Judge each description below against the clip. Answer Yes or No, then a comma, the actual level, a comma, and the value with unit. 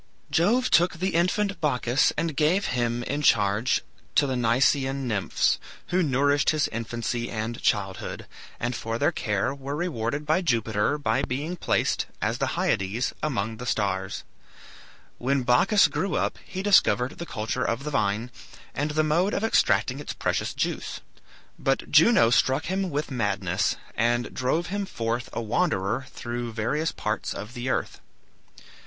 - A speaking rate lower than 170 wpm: Yes, average, 155 wpm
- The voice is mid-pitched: No, low, 130 Hz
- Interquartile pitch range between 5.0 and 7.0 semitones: Yes, average, 5.3 semitones